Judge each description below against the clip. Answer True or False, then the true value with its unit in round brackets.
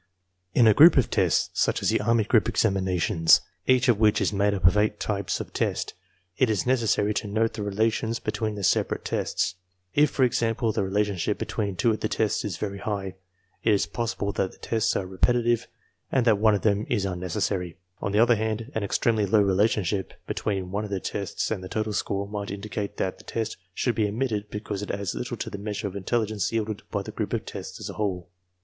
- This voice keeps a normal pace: False (220 wpm)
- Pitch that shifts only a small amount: True (2.1 semitones)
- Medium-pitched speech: False (105 Hz)